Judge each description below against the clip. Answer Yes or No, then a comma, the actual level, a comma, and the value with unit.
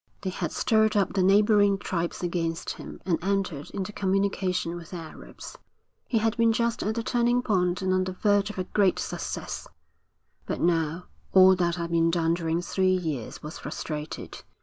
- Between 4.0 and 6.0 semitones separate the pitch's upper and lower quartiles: No, average, 3.2 semitones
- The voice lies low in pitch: No, medium, 185 Hz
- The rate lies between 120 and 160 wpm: No, average, 180 wpm